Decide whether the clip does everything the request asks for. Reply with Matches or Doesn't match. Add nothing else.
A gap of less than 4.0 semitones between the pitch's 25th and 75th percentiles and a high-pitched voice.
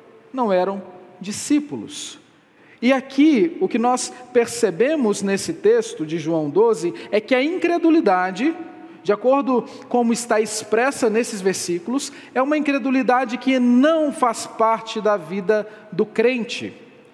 Doesn't match